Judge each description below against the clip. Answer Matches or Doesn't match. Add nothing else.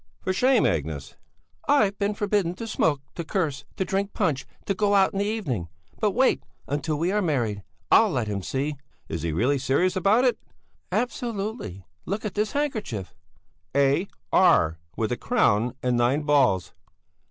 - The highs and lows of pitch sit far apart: Matches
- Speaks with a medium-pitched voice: Matches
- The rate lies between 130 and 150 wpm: Doesn't match